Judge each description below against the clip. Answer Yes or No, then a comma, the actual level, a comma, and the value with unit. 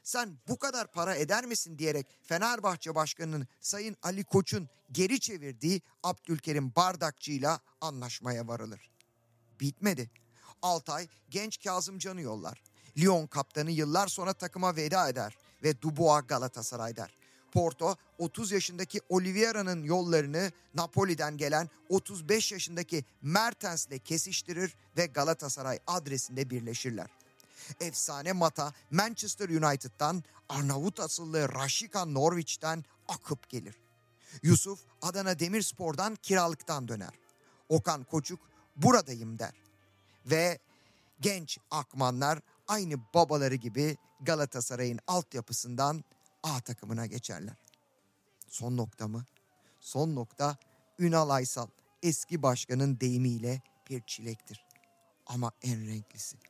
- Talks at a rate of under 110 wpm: Yes, average, 100 wpm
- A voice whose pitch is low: No, medium, 150 Hz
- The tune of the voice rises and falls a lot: Yes, wide, 5.9 semitones